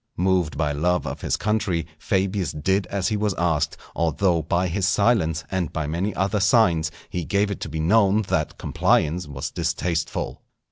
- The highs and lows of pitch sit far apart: No, average, 3.5 semitones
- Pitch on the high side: No, very low, 90 Hz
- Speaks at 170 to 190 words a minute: Yes, average, 175 wpm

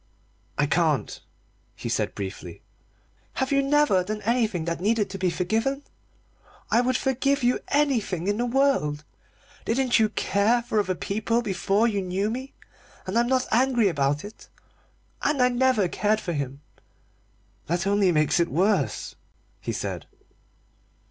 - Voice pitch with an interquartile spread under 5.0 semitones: No, average, 5.3 semitones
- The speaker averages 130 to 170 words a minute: Yes, average, 150 wpm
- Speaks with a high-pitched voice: Yes, high, 215 Hz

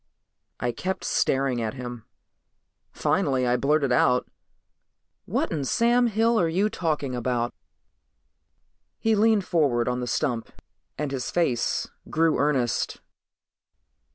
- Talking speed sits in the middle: No, slow, 120 wpm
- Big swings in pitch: Yes, wide, 6.0 semitones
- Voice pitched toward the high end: No, medium, 140 Hz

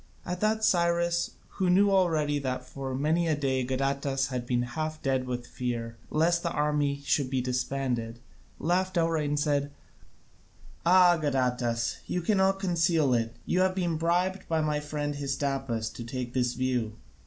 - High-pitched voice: No, medium, 145 Hz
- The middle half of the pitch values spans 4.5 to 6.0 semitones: Yes, average, 5.1 semitones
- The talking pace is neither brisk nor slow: Yes, average, 160 wpm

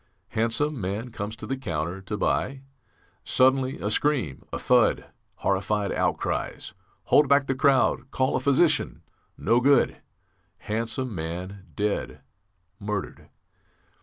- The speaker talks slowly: Yes, slow, 120 wpm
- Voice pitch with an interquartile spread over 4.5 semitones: Yes, average, 5.0 semitones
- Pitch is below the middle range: Yes, low, 115 Hz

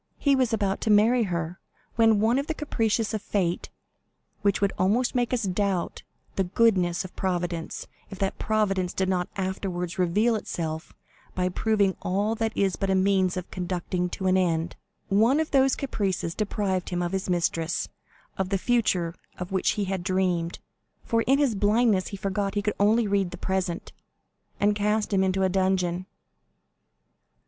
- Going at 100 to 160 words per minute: No, average, 170 wpm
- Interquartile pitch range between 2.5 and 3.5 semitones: Yes, average, 2.8 semitones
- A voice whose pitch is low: No, high, 195 Hz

